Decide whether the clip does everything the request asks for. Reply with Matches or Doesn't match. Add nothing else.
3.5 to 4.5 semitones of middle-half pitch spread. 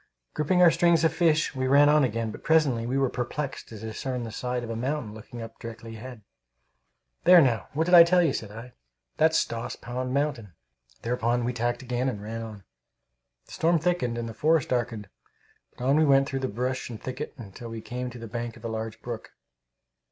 Matches